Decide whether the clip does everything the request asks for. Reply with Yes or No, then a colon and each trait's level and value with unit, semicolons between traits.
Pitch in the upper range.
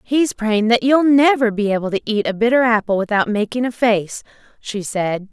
Yes: high, 225 Hz